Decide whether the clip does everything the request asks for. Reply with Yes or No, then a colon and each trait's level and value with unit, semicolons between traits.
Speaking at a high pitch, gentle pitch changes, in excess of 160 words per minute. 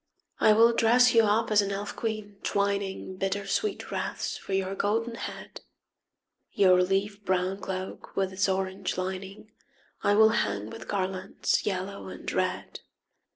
No: high, 195 Hz; narrow, 2.0 semitones; average, 145 wpm